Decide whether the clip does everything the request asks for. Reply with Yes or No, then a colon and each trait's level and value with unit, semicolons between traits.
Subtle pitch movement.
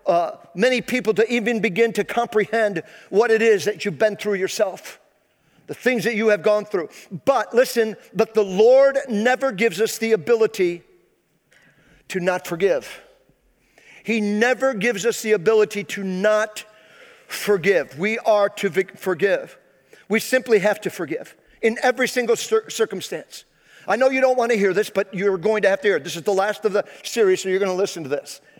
No: average, 3.1 semitones